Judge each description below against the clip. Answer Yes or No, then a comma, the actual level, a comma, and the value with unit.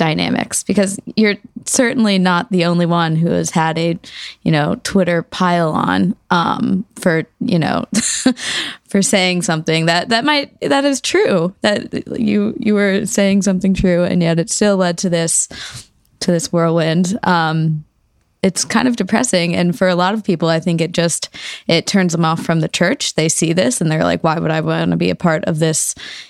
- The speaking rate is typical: Yes, average, 195 wpm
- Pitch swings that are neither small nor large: Yes, average, 3.9 semitones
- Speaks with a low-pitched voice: No, medium, 180 Hz